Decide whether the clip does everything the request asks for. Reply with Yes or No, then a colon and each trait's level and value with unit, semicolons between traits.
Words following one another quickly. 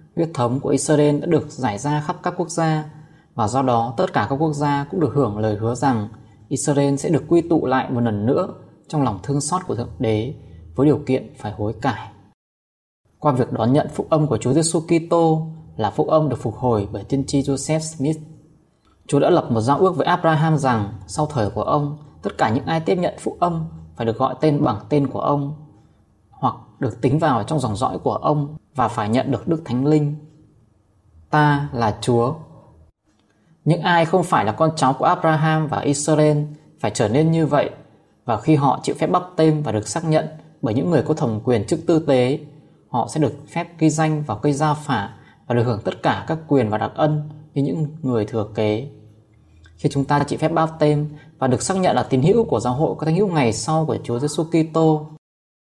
No: average, 220 wpm